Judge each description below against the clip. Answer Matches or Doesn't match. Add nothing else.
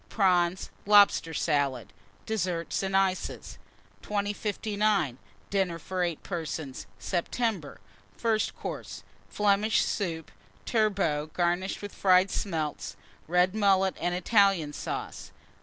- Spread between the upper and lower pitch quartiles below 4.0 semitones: Matches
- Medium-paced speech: Doesn't match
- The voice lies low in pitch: Doesn't match